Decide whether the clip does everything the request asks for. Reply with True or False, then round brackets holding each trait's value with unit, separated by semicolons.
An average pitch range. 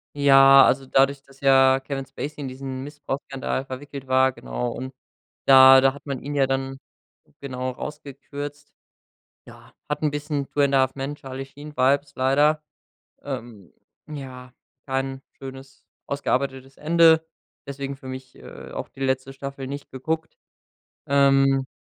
False (1.2 semitones)